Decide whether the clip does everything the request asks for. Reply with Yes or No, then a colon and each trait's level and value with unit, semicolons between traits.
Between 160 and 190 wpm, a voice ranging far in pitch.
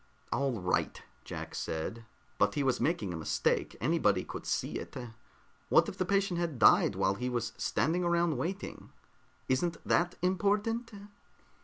No: average, 150 wpm; wide, 7.5 semitones